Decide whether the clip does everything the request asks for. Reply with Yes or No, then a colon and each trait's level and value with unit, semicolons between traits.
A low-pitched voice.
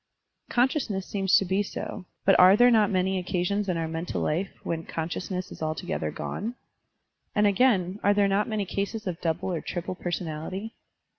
No: high, 190 Hz